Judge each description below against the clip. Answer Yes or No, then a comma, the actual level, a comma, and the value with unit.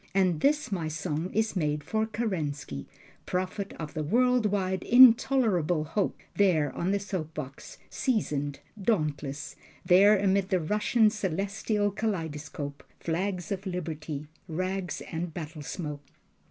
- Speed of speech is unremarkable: No, slow, 125 wpm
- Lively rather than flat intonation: No, average, 5.0 semitones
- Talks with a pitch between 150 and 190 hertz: Yes, medium, 185 Hz